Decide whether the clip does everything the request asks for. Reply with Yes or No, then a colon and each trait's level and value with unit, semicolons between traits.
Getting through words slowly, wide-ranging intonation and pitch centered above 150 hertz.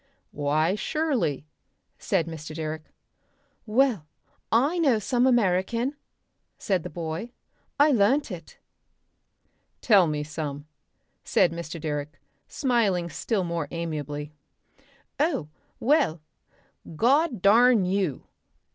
Yes: slow, 100 wpm; wide, 7.6 semitones; medium, 185 Hz